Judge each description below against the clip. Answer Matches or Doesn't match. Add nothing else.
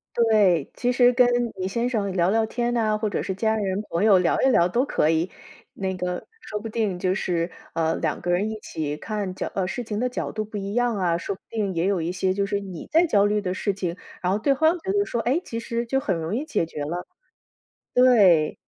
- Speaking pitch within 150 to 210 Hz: Matches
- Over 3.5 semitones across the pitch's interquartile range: Matches